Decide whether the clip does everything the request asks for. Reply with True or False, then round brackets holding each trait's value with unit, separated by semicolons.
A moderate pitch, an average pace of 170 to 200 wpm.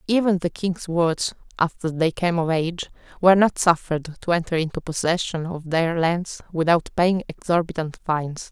False (170 Hz; 160 wpm)